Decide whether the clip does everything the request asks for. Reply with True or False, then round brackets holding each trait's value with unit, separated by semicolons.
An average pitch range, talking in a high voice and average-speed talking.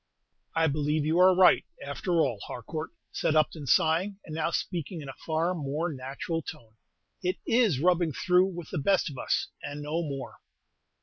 False (3.6 semitones; 160 Hz; 175 wpm)